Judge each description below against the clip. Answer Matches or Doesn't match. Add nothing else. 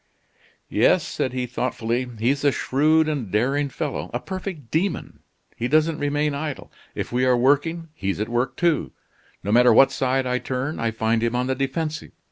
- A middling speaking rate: Matches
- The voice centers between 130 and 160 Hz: Matches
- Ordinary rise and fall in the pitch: Matches